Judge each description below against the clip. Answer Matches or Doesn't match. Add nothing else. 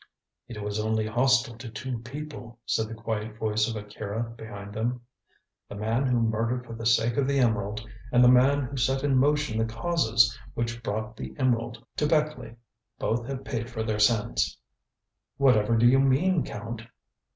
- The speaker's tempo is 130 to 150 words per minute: Doesn't match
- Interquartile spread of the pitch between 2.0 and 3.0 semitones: Matches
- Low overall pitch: Matches